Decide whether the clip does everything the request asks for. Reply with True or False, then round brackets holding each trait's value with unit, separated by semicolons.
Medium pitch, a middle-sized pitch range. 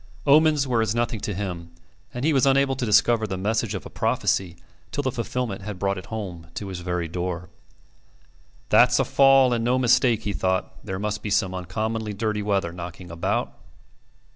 False (105 Hz; 4.6 semitones)